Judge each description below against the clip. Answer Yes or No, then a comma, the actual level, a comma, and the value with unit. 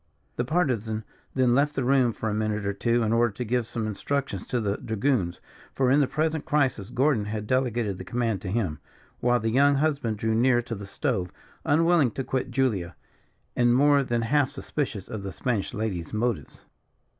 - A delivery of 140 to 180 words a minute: No, average, 190 wpm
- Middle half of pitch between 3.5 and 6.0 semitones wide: Yes, average, 3.8 semitones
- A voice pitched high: No, low, 120 Hz